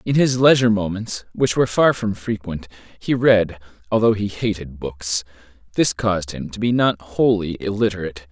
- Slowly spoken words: No, average, 165 wpm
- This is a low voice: Yes, low, 100 Hz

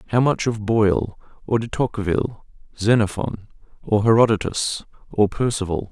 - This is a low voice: Yes, low, 110 Hz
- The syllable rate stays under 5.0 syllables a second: No, 5.2 syllables/s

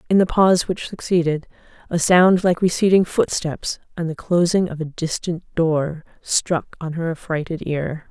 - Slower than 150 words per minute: No, average, 165 wpm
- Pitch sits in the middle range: Yes, medium, 170 Hz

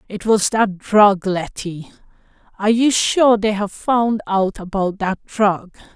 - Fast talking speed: No, average, 140 wpm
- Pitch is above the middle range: Yes, high, 205 Hz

